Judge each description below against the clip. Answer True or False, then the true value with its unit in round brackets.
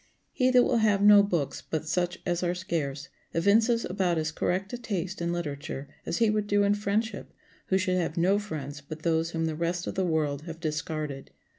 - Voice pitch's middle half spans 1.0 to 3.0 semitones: False (4.2 semitones)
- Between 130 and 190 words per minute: False (205 wpm)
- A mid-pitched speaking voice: True (175 Hz)